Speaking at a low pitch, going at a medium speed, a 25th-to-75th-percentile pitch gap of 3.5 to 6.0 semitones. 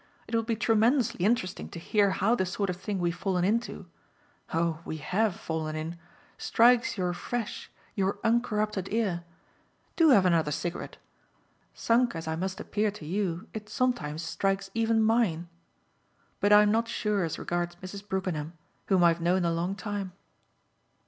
No: high, 195 Hz; average, 160 wpm; average, 4.2 semitones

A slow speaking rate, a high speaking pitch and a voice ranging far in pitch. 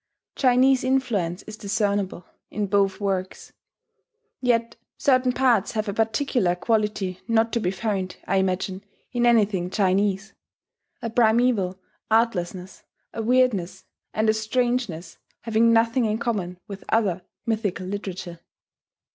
No: slow, 120 wpm; high, 215 Hz; average, 3.5 semitones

